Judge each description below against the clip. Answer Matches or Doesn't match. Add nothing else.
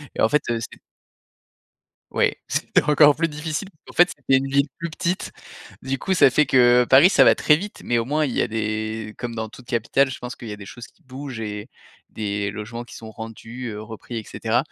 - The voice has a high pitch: Doesn't match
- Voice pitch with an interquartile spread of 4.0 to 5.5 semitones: Matches